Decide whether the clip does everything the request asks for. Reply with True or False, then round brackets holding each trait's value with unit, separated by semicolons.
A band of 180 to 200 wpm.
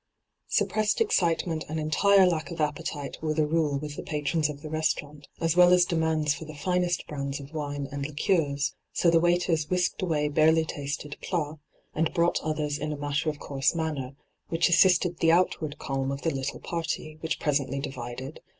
True (185 wpm)